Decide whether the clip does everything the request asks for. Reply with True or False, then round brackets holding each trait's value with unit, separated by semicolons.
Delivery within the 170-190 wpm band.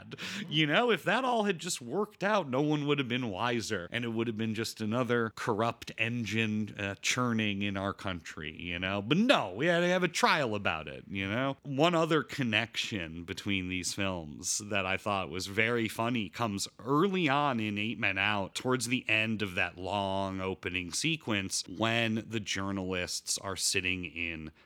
True (185 wpm)